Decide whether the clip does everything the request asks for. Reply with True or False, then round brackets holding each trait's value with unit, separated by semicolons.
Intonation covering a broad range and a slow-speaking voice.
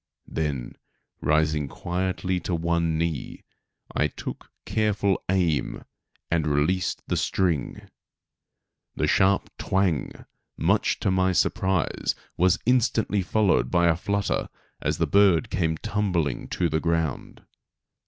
False (3.2 semitones; 115 wpm)